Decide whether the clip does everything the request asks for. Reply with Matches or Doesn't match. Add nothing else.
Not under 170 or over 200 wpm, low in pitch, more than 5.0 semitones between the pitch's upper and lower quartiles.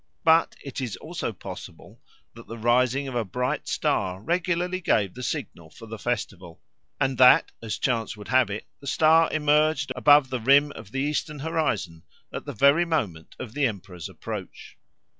Matches